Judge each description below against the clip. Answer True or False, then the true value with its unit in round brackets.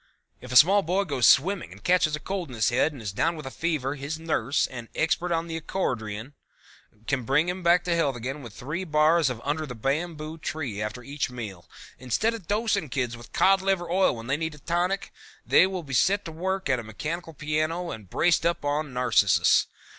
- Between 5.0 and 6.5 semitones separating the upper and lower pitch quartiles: True (5.4 semitones)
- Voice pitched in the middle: True (155 Hz)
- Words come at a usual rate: False (215 wpm)